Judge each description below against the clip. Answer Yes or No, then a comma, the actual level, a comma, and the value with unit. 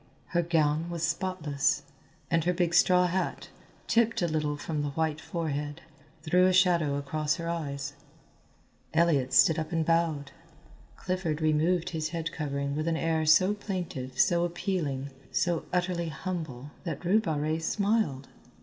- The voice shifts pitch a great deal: No, average, 2.9 semitones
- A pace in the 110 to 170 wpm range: Yes, average, 150 wpm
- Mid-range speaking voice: Yes, medium, 165 Hz